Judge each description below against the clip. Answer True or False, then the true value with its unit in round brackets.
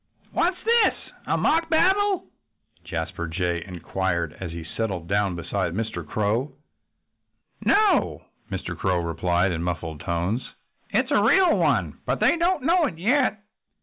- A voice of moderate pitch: False (95 Hz)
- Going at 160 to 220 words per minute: False (145 wpm)